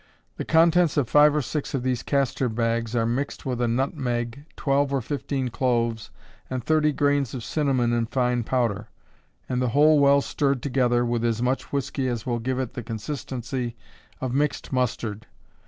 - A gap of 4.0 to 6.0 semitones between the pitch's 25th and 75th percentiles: No, average, 2.9 semitones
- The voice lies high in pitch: No, low, 125 Hz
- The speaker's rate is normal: Yes, average, 175 wpm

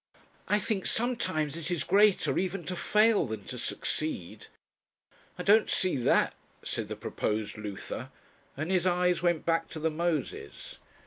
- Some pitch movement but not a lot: Yes, average, 4.1 semitones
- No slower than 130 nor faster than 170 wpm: Yes, average, 150 wpm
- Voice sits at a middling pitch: Yes, medium, 170 Hz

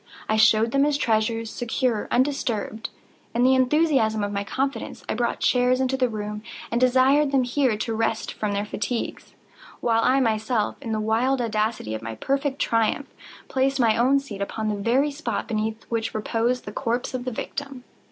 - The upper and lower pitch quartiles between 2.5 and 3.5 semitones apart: Yes, average, 3.2 semitones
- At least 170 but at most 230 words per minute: Yes, average, 180 wpm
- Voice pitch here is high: Yes, high, 235 Hz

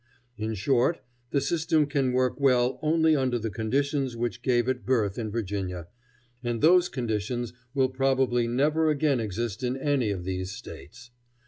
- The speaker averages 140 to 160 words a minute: Yes, average, 155 wpm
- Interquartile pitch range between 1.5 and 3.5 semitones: No, average, 3.9 semitones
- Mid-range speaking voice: No, low, 125 Hz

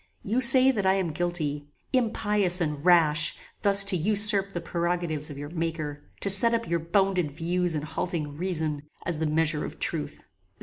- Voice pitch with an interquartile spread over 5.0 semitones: No, average, 4.2 semitones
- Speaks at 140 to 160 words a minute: No, average, 175 wpm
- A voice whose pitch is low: No, medium, 175 Hz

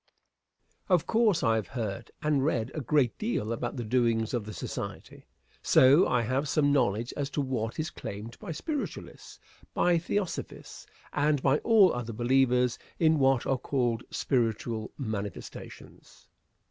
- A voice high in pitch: No, low, 130 Hz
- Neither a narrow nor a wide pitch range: Yes, average, 4.7 semitones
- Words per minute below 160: Yes, average, 150 wpm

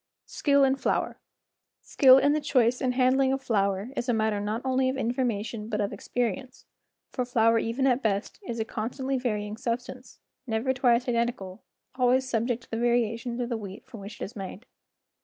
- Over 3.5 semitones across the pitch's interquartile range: No, average, 2.7 semitones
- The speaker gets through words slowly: No, average, 195 wpm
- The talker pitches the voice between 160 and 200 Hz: No, high, 240 Hz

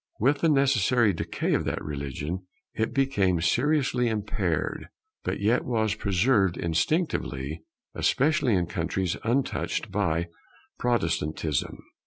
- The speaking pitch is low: Yes, low, 100 Hz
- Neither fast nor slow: No, slow, 110 wpm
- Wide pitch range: Yes, wide, 7.4 semitones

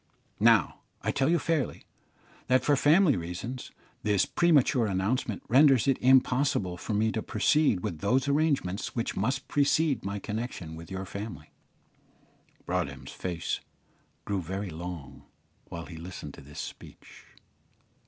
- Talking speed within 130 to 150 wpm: Yes, slow, 135 wpm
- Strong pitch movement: Yes, wide, 7.0 semitones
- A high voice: No, low, 110 Hz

